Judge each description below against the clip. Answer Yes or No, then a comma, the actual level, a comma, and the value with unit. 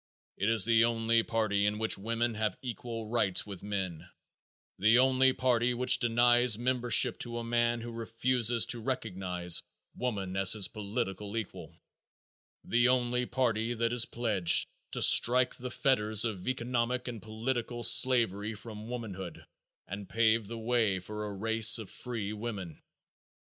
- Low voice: Yes, low, 115 Hz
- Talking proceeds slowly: No, average, 150 wpm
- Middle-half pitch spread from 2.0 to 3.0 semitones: Yes, narrow, 2.4 semitones